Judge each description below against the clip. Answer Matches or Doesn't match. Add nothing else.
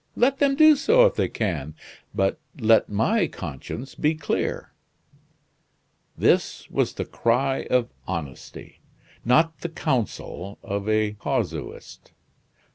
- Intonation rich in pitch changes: Matches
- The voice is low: Matches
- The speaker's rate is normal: Doesn't match